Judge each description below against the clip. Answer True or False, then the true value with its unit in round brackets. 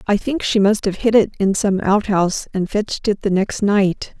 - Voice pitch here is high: True (200 Hz)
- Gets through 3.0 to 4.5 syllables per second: False (4.9 syllables/s)